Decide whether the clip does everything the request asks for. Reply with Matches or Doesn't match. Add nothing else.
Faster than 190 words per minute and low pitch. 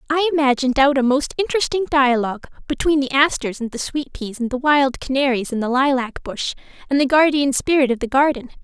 Doesn't match